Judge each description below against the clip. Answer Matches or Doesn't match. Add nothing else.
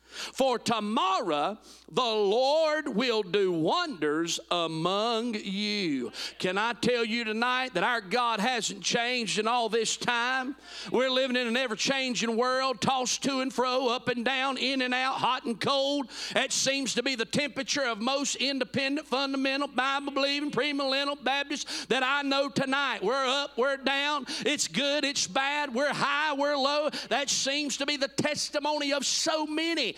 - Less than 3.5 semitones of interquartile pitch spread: Matches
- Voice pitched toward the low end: Doesn't match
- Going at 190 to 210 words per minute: Doesn't match